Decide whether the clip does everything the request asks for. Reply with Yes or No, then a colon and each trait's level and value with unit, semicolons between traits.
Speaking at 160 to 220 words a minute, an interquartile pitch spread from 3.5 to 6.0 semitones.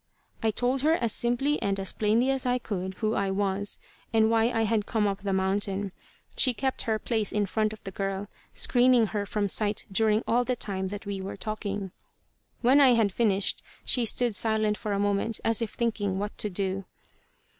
No: average, 200 wpm; average, 2.7 semitones